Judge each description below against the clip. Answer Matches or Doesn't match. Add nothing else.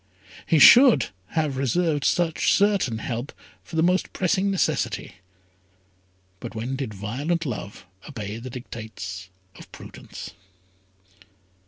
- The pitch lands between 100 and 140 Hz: Matches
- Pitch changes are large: Matches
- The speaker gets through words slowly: Matches